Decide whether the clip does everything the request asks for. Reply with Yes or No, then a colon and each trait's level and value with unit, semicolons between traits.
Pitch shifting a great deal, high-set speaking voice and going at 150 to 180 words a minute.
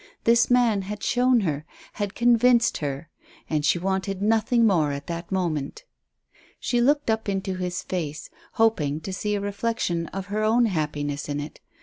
Yes: wide, 6.0 semitones; high, 195 Hz; average, 165 wpm